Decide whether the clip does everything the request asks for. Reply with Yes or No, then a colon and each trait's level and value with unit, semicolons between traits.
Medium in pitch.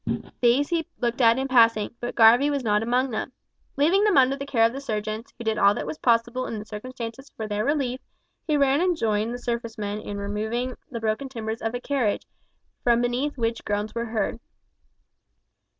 No: high, 235 Hz